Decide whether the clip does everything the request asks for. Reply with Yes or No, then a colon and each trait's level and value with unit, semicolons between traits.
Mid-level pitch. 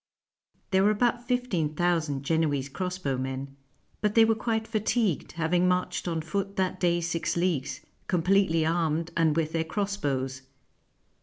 Yes: medium, 170 Hz